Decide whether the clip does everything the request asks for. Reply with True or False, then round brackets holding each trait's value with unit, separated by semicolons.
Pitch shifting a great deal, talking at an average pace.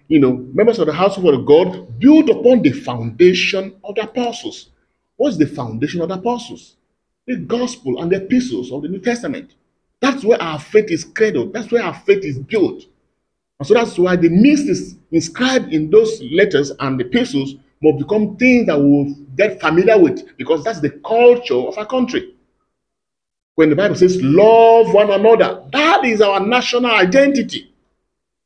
True (7.4 semitones; 175 wpm)